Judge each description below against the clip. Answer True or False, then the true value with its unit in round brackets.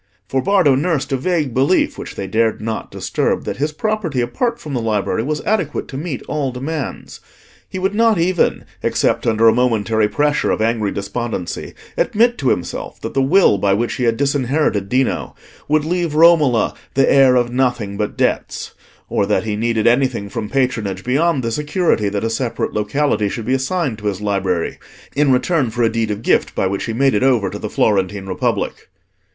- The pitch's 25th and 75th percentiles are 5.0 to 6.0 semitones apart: True (5.4 semitones)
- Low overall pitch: True (125 Hz)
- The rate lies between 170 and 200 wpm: True (190 wpm)